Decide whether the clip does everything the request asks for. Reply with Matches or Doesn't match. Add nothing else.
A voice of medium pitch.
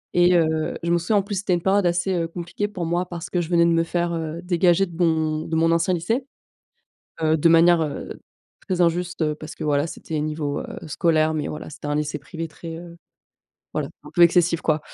Matches